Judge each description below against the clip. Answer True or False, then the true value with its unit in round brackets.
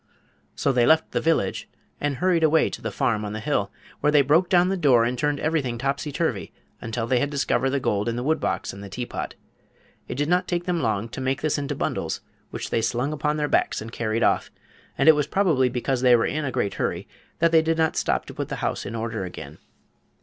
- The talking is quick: True (240 wpm)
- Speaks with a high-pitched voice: False (135 Hz)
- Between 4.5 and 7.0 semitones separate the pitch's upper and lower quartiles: True (5.1 semitones)